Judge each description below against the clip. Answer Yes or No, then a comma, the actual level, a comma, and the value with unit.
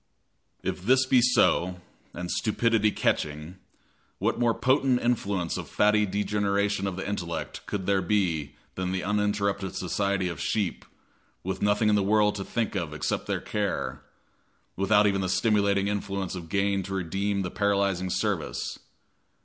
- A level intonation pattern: Yes, narrow, 2.1 semitones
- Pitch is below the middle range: Yes, low, 100 Hz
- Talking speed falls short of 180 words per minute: Yes, average, 150 wpm